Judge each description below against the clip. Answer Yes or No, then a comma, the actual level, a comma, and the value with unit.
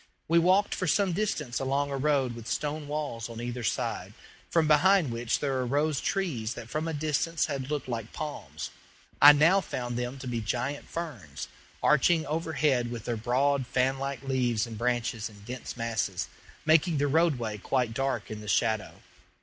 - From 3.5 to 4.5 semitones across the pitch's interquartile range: Yes, average, 4.2 semitones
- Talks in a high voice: No, low, 135 Hz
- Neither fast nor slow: Yes, average, 175 wpm